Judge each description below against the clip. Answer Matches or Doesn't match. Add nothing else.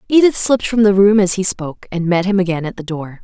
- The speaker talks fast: Matches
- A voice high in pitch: Matches